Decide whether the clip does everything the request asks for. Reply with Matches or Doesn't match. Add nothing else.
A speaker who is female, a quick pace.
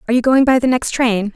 Matches